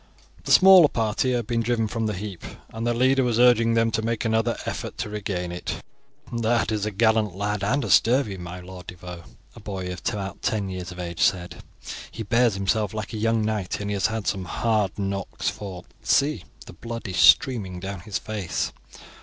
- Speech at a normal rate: No, fast, 210 wpm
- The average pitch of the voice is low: Yes, low, 105 Hz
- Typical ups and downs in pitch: Yes, average, 3.3 semitones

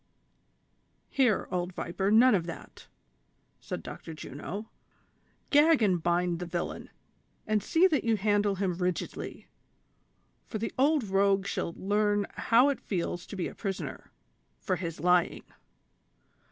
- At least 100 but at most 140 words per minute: Yes, slow, 135 wpm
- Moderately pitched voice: No, high, 195 Hz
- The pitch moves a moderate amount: Yes, average, 3.7 semitones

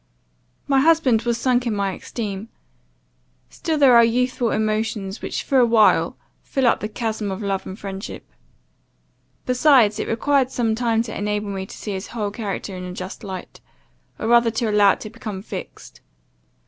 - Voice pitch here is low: No, high, 220 Hz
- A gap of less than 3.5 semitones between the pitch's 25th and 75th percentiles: Yes, average, 3.1 semitones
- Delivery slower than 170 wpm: No, average, 175 wpm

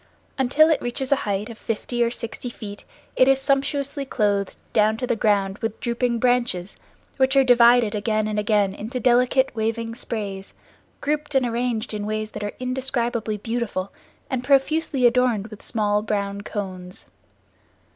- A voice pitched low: No, high, 235 Hz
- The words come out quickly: No, average, 155 wpm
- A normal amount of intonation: Yes, average, 3.3 semitones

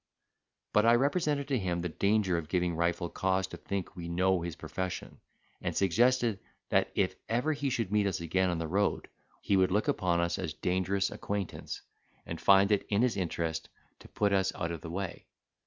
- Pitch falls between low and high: No, very low, 95 Hz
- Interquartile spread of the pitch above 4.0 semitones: No, average, 3.3 semitones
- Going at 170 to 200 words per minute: Yes, average, 190 wpm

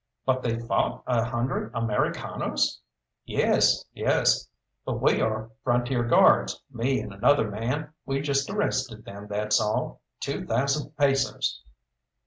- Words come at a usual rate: No, slow, 125 wpm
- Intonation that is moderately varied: Yes, average, 3.7 semitones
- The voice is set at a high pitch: No, low, 120 Hz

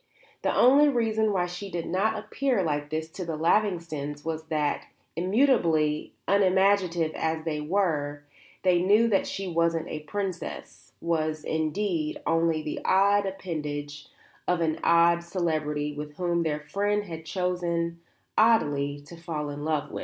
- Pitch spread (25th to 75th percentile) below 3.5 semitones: No, average, 3.8 semitones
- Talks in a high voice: No, medium, 170 Hz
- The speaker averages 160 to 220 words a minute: No, average, 145 wpm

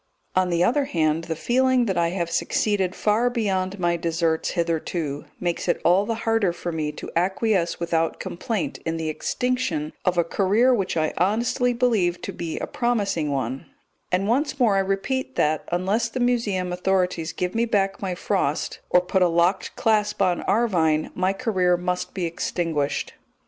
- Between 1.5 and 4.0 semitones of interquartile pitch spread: No, average, 4.6 semitones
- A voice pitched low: No, medium, 185 Hz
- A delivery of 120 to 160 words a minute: No, average, 175 wpm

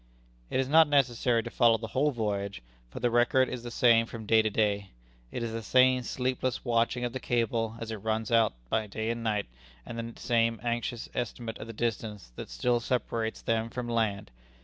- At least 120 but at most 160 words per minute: No, average, 200 wpm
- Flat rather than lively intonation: Yes, narrow, 1.6 semitones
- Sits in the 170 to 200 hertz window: No, low, 115 Hz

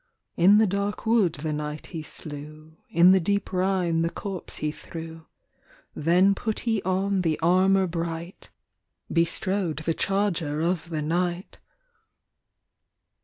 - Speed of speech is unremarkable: No, slow, 130 wpm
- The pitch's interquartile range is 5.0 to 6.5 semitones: No, average, 3.2 semitones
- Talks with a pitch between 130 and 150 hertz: No, medium, 175 Hz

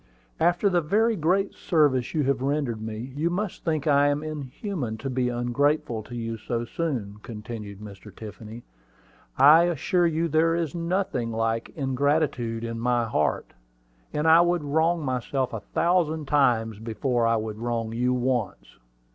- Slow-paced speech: No, average, 155 wpm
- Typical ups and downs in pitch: No, wide, 5.8 semitones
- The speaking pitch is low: Yes, low, 130 Hz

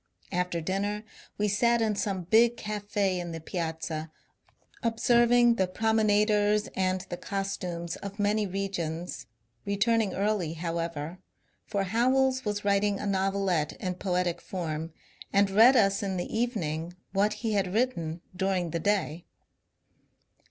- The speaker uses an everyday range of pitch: Yes, average, 3.2 semitones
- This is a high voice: Yes, high, 195 Hz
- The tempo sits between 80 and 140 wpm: Yes, slow, 135 wpm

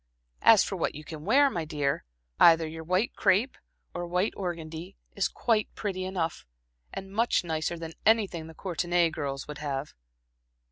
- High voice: No, medium, 170 Hz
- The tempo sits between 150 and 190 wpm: Yes, average, 160 wpm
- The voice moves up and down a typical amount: Yes, average, 3.4 semitones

